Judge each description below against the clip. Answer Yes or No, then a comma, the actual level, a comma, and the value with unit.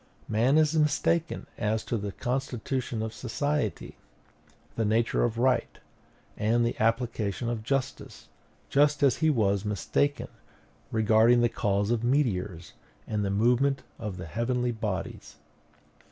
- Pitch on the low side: Yes, low, 115 Hz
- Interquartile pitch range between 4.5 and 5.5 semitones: No, average, 3.6 semitones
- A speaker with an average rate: No, slow, 130 wpm